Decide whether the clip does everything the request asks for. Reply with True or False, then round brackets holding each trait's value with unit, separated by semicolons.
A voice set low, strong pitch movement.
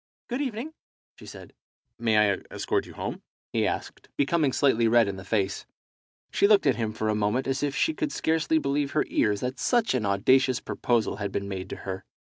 True (125 Hz; 6.3 semitones)